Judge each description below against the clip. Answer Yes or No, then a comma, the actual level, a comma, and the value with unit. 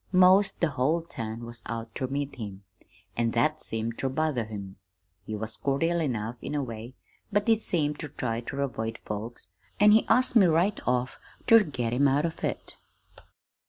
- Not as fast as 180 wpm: No, average, 185 wpm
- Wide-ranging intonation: Yes, wide, 6.2 semitones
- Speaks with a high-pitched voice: No, low, 130 Hz